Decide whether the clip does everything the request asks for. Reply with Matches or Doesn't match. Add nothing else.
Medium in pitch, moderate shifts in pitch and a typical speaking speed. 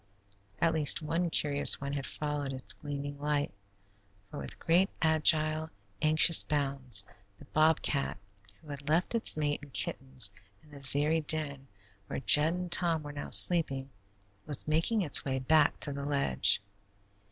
Doesn't match